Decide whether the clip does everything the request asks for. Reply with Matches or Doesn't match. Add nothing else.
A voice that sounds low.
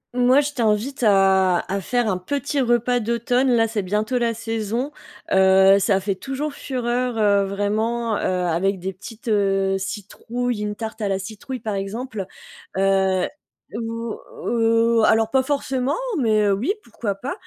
Doesn't match